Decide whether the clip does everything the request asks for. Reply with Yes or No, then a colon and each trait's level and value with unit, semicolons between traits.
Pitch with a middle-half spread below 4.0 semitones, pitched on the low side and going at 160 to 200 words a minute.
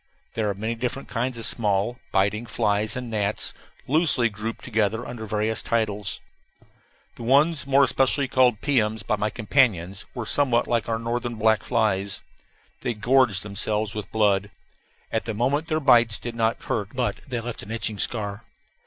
Yes: average, 2.7 semitones; low, 115 Hz; average, 165 wpm